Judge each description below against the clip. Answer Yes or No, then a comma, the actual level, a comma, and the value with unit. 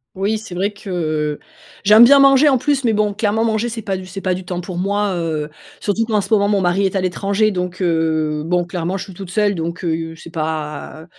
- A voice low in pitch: No, high, 190 Hz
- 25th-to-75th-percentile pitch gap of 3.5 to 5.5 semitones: Yes, average, 3.8 semitones